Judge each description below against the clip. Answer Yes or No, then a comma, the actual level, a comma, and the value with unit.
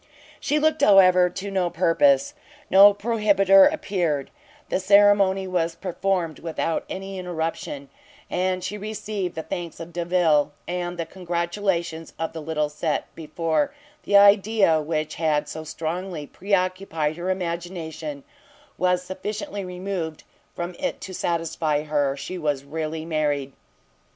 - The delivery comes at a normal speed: No, slow, 130 wpm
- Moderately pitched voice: Yes, medium, 175 Hz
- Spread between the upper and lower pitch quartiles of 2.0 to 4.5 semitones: Yes, average, 3.4 semitones